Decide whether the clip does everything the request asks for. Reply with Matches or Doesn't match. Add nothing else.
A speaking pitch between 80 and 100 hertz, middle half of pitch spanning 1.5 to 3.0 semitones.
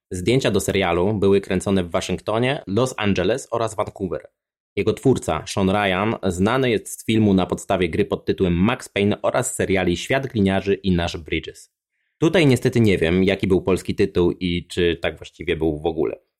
Matches